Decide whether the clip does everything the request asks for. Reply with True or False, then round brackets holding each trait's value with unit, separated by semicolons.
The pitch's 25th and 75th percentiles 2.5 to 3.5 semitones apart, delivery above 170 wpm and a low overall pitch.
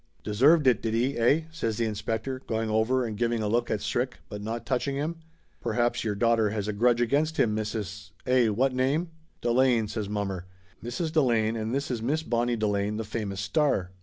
True (3.2 semitones; 195 wpm; 115 Hz)